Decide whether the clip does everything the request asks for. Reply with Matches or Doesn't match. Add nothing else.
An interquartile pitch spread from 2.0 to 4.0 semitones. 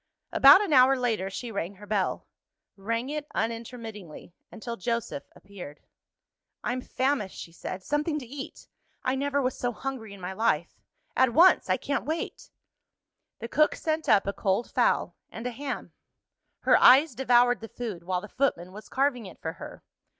Doesn't match